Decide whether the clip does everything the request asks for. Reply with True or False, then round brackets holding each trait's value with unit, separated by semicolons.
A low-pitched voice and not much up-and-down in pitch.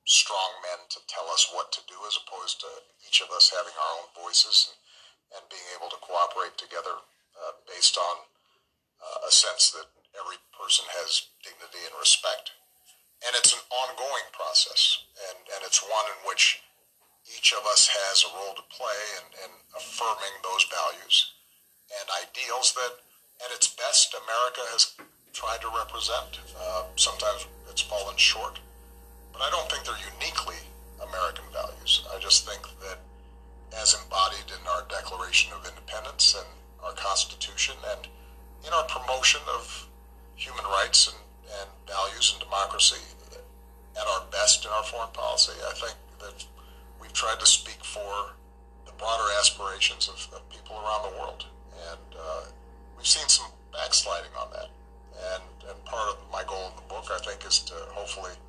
True (65 Hz; 0.9 semitones)